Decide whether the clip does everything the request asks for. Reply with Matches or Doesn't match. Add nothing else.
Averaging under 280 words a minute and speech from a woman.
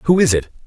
Doesn't match